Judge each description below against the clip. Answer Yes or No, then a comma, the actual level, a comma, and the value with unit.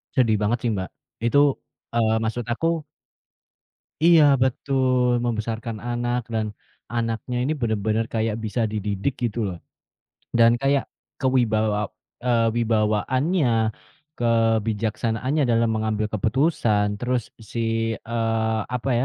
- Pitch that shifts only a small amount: Yes, narrow, 2.2 semitones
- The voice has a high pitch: No, low, 115 Hz